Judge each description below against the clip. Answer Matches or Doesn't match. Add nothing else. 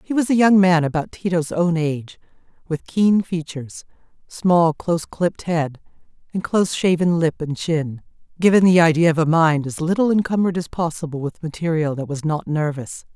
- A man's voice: Doesn't match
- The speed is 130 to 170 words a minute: Doesn't match